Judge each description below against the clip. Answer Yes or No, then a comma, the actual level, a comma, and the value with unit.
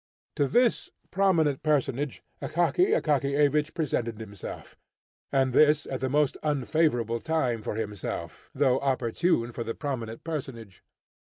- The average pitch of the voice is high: No, medium, 140 Hz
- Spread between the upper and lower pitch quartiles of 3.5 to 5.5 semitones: Yes, average, 4.5 semitones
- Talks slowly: Yes, slow, 120 wpm